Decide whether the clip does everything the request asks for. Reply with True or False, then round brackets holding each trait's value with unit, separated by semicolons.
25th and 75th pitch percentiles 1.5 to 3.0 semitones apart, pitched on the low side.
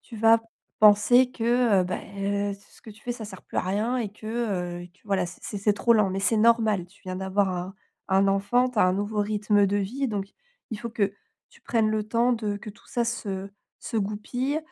False (2.7 semitones; 210 Hz)